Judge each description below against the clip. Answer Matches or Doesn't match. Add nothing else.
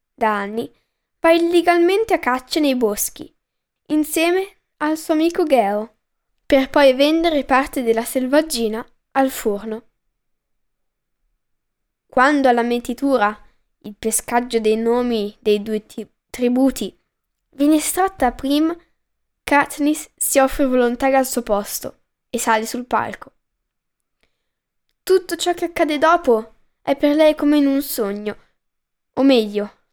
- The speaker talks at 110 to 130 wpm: Matches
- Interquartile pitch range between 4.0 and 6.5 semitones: Matches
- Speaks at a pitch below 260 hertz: Doesn't match